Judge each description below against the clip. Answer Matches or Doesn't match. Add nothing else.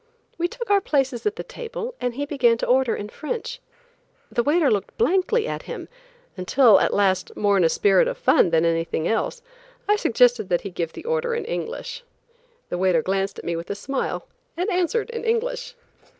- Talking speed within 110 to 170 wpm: Doesn't match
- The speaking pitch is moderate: Doesn't match